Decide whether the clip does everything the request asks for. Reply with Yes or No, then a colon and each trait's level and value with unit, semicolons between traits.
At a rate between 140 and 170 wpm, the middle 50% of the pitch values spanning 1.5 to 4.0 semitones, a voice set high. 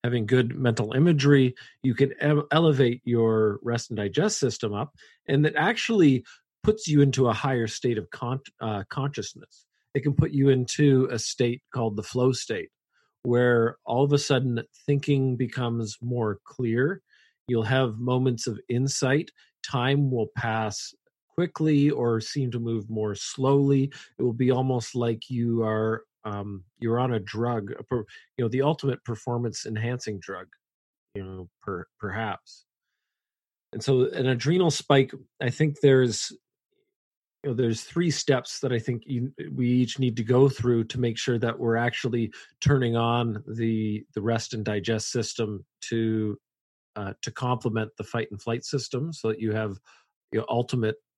No: average, 160 wpm; average, 3.2 semitones; low, 125 Hz